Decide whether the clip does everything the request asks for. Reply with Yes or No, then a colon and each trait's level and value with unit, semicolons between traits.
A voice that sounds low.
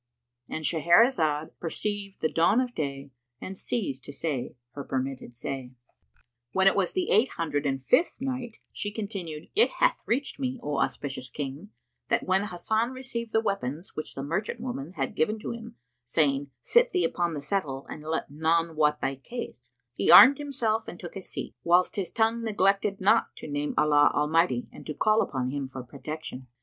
No: medium, 170 Hz